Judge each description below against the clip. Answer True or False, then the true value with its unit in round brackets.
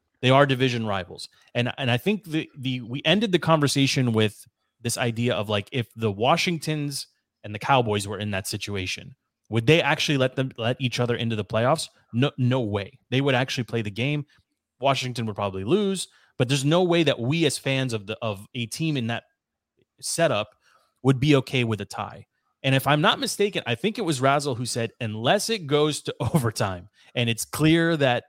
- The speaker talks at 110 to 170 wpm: False (205 wpm)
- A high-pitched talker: False (130 Hz)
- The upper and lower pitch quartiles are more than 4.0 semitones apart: True (4.4 semitones)